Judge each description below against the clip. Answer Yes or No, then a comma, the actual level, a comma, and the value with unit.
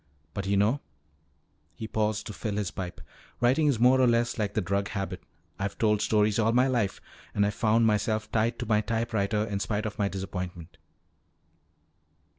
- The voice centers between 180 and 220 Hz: No, low, 105 Hz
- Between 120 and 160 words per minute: No, average, 180 wpm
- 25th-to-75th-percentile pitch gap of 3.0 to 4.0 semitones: No, narrow, 2.4 semitones